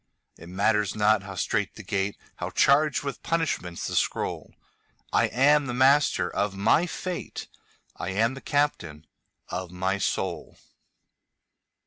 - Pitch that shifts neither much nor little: No, wide, 6.7 semitones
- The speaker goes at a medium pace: No, slow, 120 wpm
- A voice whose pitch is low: Yes, low, 105 Hz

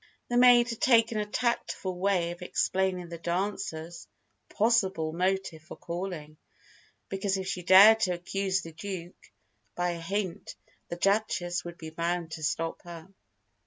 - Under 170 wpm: Yes, average, 150 wpm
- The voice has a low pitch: No, medium, 185 Hz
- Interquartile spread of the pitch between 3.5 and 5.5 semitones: No, average, 2.7 semitones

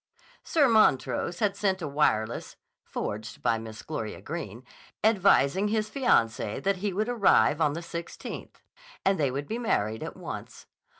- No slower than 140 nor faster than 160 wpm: Yes, average, 155 wpm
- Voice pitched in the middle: Yes, medium, 170 Hz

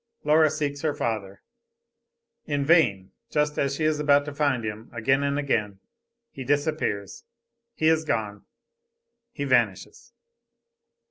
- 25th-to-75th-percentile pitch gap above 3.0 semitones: Yes, average, 5.2 semitones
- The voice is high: No, medium, 140 Hz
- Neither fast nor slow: No, slow, 130 wpm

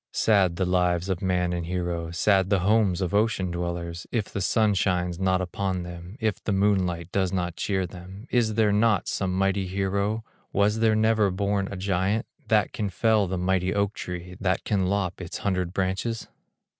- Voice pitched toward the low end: Yes, very low, 95 Hz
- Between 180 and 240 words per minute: Yes, average, 185 wpm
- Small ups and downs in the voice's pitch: Yes, narrow, 2.3 semitones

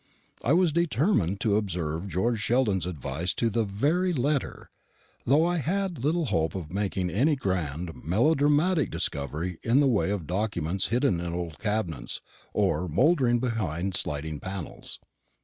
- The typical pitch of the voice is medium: No, low, 105 Hz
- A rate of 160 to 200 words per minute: No, average, 145 wpm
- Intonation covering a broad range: Yes, wide, 8.3 semitones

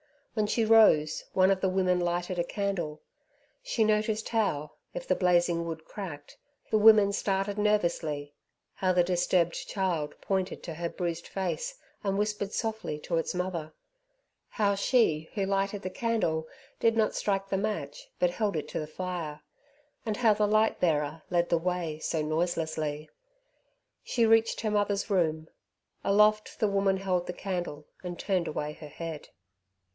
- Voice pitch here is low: No, medium, 185 Hz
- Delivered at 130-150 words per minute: No, average, 160 wpm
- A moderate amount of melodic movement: Yes, average, 4.2 semitones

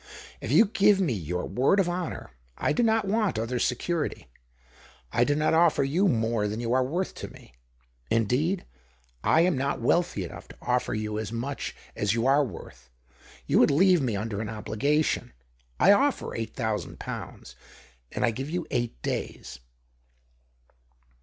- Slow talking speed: No, average, 170 wpm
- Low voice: Yes, low, 130 Hz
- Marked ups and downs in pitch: Yes, wide, 7.8 semitones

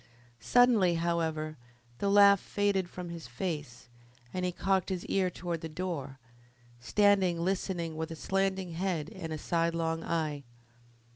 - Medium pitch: Yes, medium, 170 Hz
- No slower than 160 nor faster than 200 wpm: No, average, 140 wpm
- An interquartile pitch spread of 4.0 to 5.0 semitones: No, average, 2.8 semitones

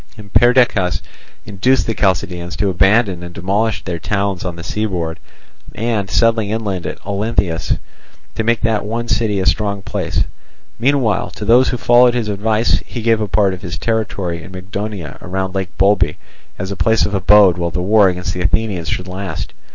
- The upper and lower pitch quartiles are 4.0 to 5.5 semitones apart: No, average, 3.6 semitones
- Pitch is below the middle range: Yes, low, 100 Hz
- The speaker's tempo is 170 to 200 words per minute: Yes, average, 180 wpm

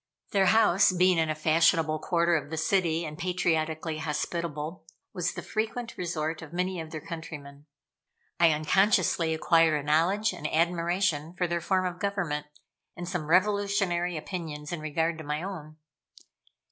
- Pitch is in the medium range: Yes, medium, 170 Hz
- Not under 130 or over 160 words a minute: Yes, average, 155 wpm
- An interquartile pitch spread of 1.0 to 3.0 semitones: Yes, average, 2.7 semitones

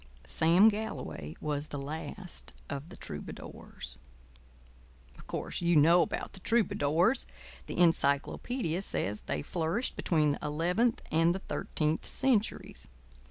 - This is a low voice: No, medium, 165 Hz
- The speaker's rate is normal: No, slow, 120 wpm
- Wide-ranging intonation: No, average, 4.9 semitones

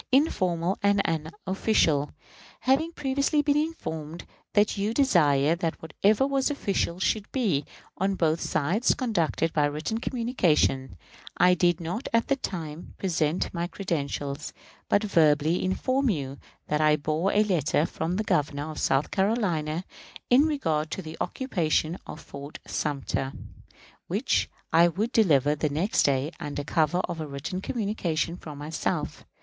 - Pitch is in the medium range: Yes, medium, 170 Hz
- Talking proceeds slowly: No, average, 145 wpm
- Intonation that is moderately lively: No, wide, 5.8 semitones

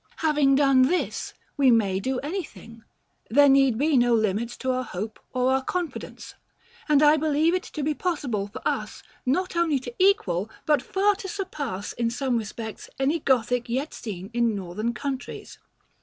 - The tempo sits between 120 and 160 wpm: No, average, 170 wpm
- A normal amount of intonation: Yes, average, 4.7 semitones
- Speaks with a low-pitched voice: No, very high, 265 Hz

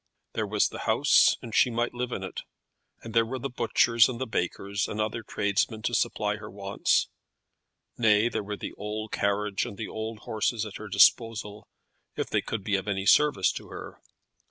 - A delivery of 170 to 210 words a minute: Yes, average, 195 wpm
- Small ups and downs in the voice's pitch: Yes, narrow, 2.3 semitones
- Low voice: Yes, low, 110 Hz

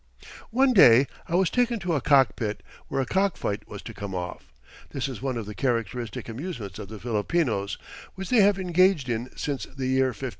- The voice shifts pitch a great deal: Yes, wide, 8.0 semitones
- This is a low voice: Yes, low, 130 Hz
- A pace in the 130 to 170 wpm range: No, average, 195 wpm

